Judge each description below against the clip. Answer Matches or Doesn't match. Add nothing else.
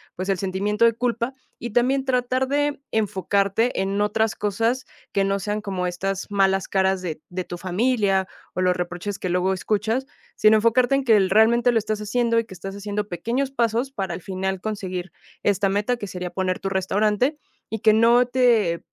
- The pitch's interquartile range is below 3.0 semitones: Doesn't match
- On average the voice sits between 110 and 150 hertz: Doesn't match